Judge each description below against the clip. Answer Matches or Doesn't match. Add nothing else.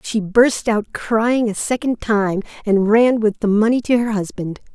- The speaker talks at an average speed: Matches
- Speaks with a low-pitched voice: Doesn't match